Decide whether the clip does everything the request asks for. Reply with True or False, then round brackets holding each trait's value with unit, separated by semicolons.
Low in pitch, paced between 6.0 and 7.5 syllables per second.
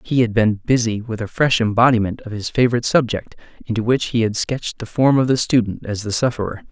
True (115 Hz; 6.1 syllables/s)